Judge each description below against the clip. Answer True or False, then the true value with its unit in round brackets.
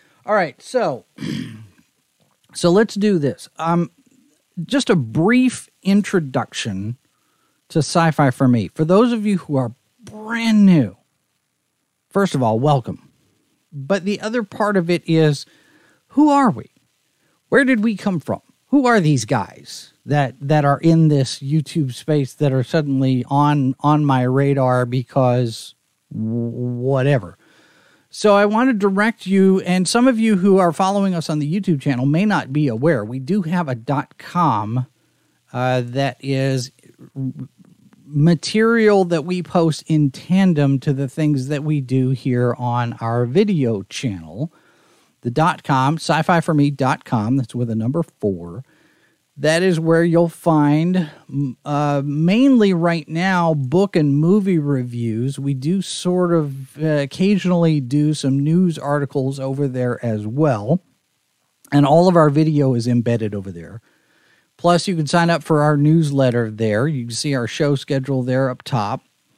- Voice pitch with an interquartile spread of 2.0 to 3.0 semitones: False (5.2 semitones)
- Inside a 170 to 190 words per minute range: False (150 wpm)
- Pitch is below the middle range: False (150 Hz)